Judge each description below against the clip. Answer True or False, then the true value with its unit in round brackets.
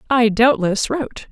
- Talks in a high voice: True (235 Hz)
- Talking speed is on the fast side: False (135 wpm)